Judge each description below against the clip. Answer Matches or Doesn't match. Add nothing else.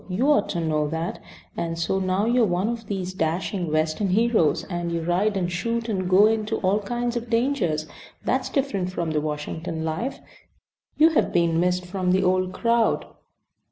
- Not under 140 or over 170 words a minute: Doesn't match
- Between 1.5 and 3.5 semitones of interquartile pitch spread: Doesn't match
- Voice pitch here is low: Doesn't match